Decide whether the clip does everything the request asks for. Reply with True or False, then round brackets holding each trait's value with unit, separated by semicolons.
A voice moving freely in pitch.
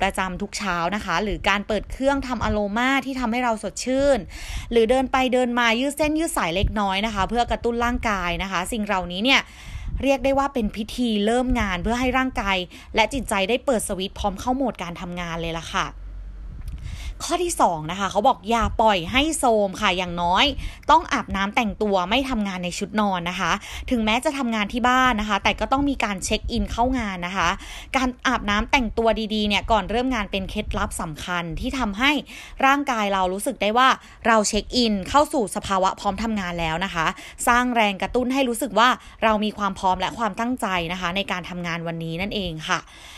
False (4.8 semitones)